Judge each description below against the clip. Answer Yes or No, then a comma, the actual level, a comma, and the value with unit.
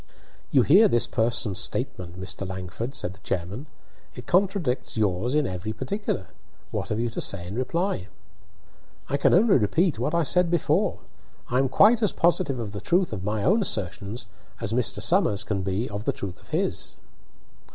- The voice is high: No, low, 120 Hz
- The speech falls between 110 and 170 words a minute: No, average, 180 wpm